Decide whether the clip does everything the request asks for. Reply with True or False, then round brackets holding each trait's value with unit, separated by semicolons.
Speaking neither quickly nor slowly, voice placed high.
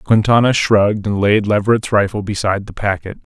False (160 wpm; 105 Hz)